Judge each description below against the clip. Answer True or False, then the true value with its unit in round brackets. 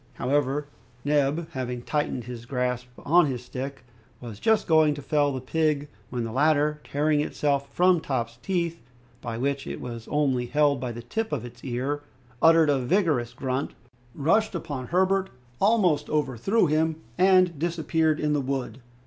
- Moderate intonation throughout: True (4.1 semitones)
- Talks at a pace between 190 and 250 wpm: False (160 wpm)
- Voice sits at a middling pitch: True (145 Hz)